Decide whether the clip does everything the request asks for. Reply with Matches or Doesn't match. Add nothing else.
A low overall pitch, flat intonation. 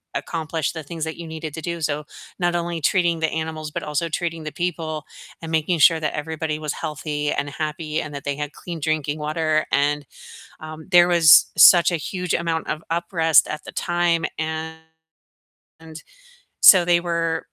Doesn't match